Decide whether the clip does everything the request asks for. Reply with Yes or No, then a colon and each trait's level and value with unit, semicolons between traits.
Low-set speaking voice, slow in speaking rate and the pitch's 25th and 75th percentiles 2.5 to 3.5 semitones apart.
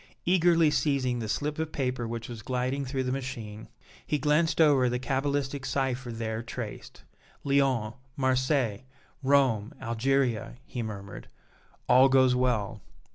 Yes: low, 130 Hz; slow, 130 wpm; average, 2.9 semitones